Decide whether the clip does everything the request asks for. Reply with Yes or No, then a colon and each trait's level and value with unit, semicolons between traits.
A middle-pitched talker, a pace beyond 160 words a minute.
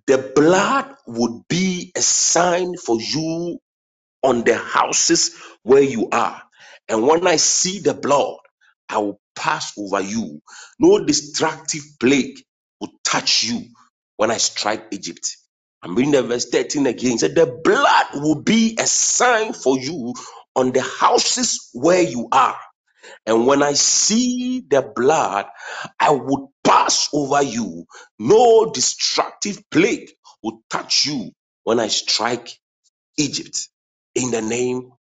No: medium, 170 Hz; average, 140 wpm